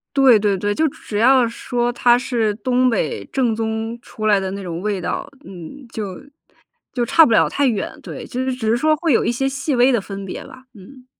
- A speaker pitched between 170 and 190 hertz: No, high, 235 Hz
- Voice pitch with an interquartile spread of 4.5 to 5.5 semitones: No, average, 3.9 semitones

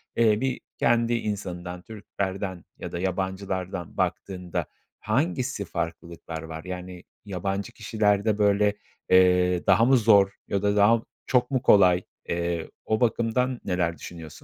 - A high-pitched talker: No, low, 100 Hz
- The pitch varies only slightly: No, average, 3.5 semitones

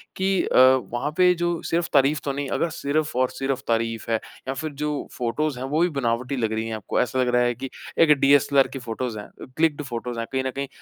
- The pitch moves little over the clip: No, average, 3.7 semitones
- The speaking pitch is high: No, low, 135 Hz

